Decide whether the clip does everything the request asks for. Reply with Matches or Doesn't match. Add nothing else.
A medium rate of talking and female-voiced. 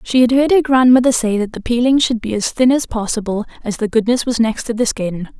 Doesn't match